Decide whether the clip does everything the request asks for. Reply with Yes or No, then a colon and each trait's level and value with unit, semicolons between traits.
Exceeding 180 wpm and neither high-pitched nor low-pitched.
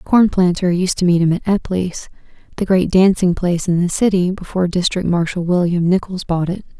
No: average, 175 wpm; medium, 180 Hz